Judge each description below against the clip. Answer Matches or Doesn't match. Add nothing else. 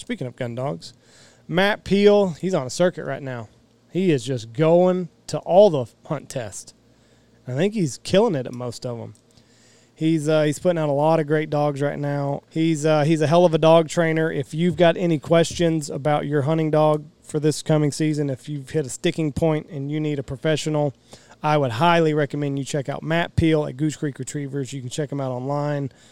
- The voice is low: Doesn't match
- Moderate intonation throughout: Matches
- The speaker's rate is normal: Doesn't match